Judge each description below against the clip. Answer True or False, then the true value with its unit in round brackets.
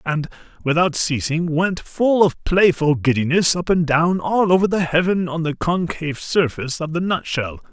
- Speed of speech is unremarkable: True (170 wpm)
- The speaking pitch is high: False (165 Hz)